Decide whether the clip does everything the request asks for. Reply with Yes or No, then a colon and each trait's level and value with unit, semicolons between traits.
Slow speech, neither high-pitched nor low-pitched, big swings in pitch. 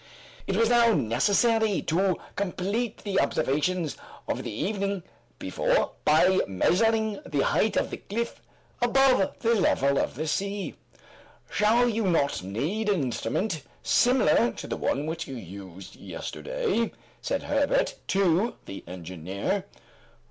No: slow, 130 wpm; high, 195 Hz; wide, 8.1 semitones